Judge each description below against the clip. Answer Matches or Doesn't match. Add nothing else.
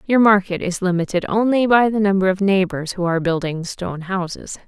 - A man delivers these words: Doesn't match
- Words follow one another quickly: Doesn't match